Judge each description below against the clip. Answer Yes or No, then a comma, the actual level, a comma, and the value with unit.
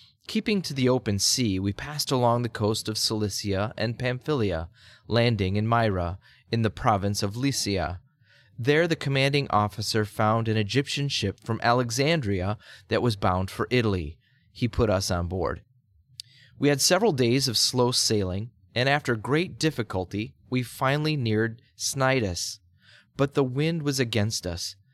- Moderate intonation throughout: Yes, average, 4.3 semitones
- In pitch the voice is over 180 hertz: No, low, 115 Hz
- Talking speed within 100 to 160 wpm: Yes, average, 150 wpm